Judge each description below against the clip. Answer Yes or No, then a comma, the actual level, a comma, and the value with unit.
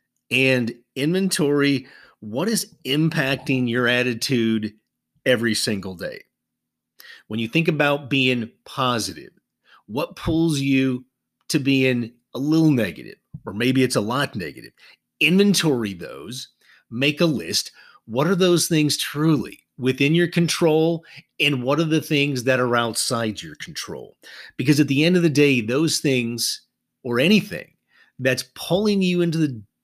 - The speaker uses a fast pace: No, average, 140 wpm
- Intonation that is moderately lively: Yes, average, 4.7 semitones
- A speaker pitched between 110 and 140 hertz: Yes, low, 135 Hz